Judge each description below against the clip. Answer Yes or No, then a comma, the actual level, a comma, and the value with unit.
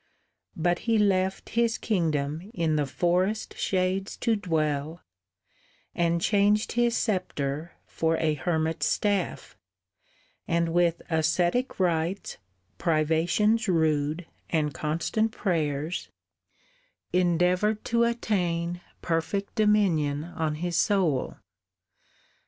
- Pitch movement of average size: Yes, average, 4.0 semitones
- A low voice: No, medium, 175 Hz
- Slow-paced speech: Yes, slow, 95 wpm